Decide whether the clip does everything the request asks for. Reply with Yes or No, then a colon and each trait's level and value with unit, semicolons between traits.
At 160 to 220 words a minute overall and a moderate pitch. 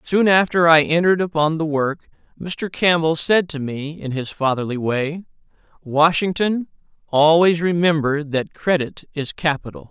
No: average, 140 wpm; medium, 160 Hz